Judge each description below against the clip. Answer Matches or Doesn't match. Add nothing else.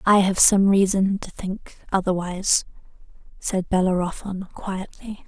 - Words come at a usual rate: Doesn't match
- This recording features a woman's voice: Matches